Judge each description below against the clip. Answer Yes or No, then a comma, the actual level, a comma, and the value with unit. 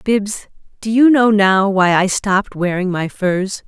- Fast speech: No, average, 180 wpm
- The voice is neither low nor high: No, high, 200 Hz